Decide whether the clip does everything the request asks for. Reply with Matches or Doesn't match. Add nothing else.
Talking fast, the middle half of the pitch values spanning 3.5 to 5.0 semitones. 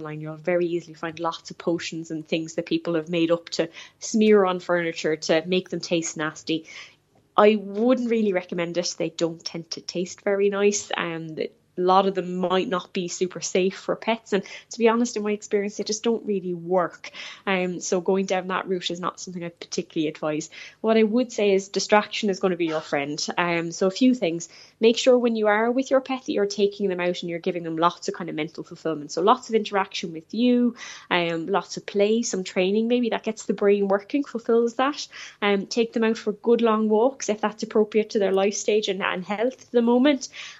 Matches